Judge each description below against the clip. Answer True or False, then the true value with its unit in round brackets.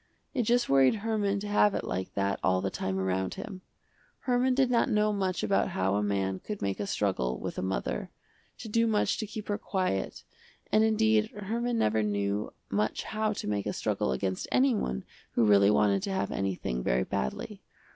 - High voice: False (135 Hz)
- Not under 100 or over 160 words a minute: False (195 wpm)